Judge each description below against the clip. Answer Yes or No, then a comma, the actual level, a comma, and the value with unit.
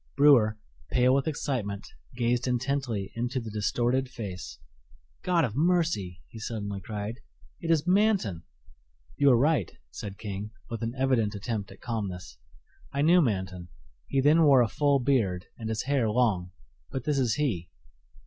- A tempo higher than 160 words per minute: No, average, 155 wpm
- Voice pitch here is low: Yes, low, 120 Hz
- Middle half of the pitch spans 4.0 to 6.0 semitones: Yes, average, 5.2 semitones